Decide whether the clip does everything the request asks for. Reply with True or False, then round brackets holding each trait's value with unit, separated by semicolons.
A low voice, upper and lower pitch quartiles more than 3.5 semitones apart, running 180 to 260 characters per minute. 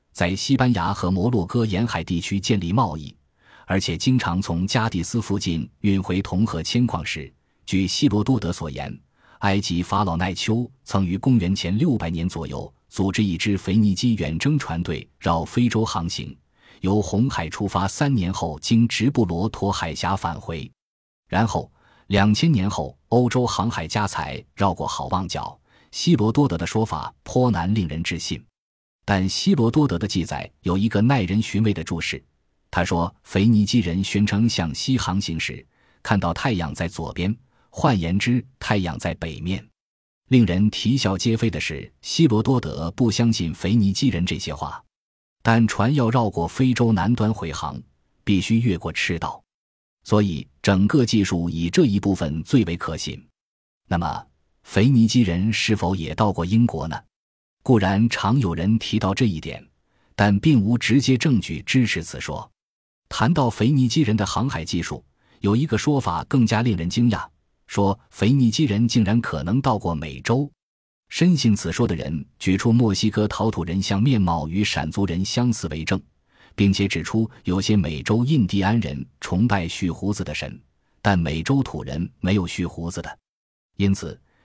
True (100 Hz; 5.3 semitones; 245 characters per minute)